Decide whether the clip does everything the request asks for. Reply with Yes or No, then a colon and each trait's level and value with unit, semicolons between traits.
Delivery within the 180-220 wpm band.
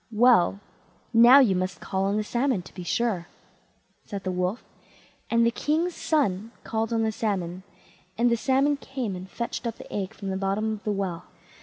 Yes: average, 190 wpm